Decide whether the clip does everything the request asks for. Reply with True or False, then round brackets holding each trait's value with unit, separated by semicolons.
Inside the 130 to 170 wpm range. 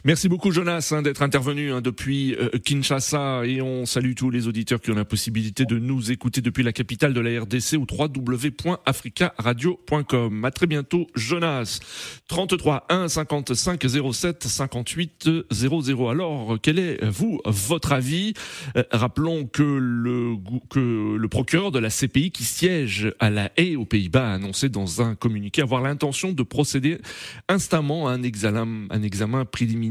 True (160 wpm)